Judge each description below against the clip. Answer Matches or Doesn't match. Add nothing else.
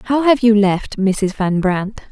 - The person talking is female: Matches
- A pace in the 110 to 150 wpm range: Doesn't match